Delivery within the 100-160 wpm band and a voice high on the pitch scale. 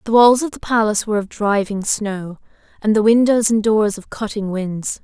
No: fast, 205 wpm; high, 215 Hz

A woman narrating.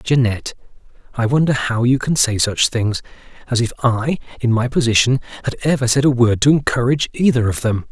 No: male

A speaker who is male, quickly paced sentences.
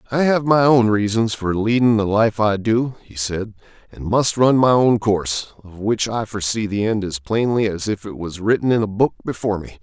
Yes: male; fast, 225 wpm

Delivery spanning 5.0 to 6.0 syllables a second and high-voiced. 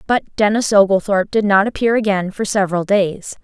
Yes: 5.5 syllables/s; high, 200 Hz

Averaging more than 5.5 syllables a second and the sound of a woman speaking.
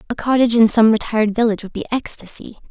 Yes: 7.3 syllables/s; female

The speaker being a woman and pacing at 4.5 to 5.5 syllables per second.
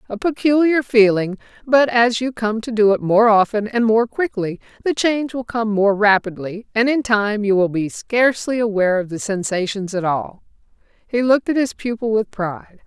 Yes: female; 5.1 syllables/s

